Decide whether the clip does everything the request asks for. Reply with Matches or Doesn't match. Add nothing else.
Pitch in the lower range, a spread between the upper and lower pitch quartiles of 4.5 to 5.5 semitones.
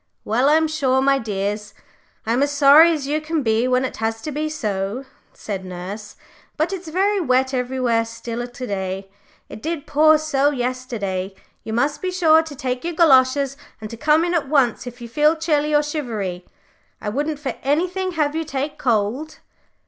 Doesn't match